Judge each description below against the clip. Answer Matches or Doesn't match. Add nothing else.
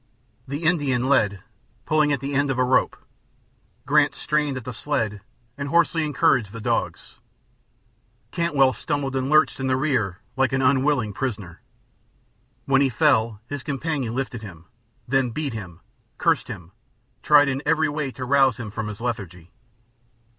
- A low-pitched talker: Matches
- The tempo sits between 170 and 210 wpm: Doesn't match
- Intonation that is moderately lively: Matches